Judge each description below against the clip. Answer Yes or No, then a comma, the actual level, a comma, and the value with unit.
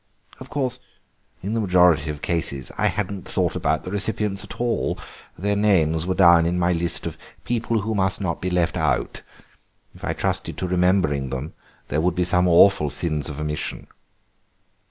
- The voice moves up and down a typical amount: Yes, average, 3.8 semitones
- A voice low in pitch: Yes, very low, 90 Hz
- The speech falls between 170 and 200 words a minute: Yes, average, 175 wpm